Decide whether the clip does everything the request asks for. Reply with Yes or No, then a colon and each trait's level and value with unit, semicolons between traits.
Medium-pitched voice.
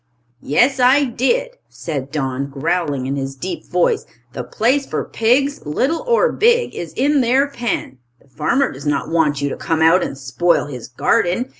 Yes: medium, 175 Hz